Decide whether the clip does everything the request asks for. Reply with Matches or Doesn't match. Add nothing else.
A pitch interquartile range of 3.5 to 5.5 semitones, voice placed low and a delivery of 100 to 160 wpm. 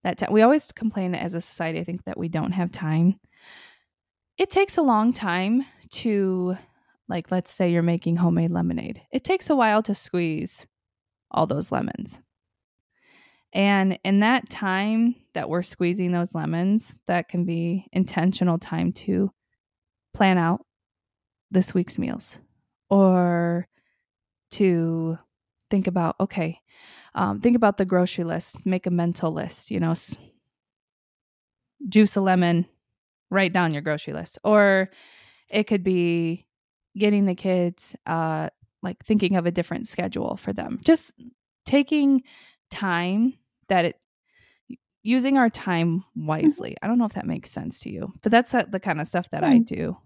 Doesn't match